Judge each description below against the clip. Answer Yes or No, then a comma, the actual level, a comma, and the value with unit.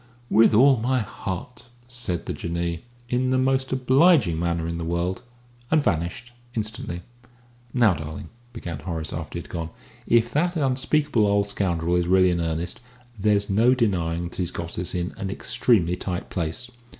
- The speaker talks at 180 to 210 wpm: No, average, 165 wpm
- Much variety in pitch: Yes, wide, 6.3 semitones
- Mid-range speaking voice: No, very low, 95 Hz